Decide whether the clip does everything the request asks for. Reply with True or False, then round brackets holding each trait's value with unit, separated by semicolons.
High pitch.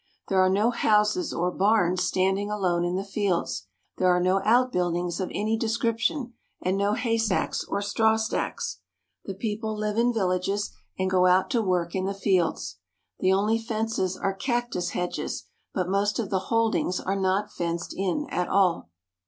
True (195 Hz)